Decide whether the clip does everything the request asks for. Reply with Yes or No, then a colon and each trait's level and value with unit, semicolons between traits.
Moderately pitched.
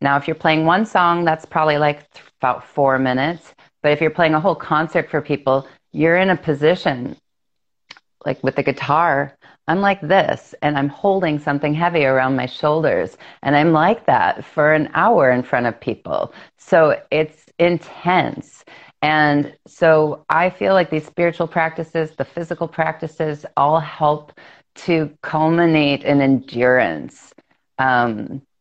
Yes: medium, 155 Hz